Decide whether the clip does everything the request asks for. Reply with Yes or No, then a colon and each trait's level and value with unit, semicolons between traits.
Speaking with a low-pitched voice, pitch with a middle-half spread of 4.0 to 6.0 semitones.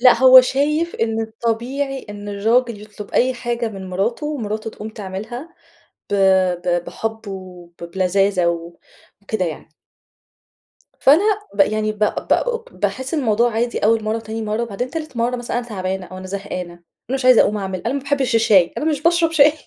No: high, 225 Hz; average, 4.5 semitones